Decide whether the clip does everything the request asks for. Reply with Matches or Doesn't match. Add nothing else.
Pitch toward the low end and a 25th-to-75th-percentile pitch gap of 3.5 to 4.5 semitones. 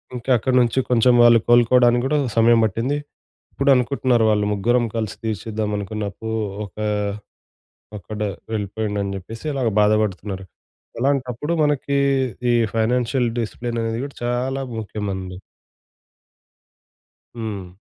Doesn't match